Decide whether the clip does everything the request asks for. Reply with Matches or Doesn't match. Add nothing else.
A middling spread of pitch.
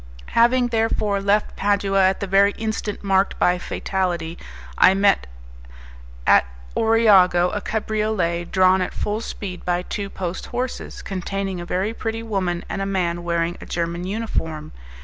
Matches